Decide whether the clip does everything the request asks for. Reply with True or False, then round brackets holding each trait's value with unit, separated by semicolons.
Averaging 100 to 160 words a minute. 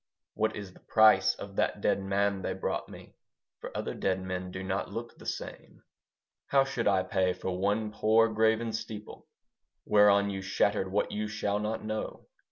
False (175 wpm)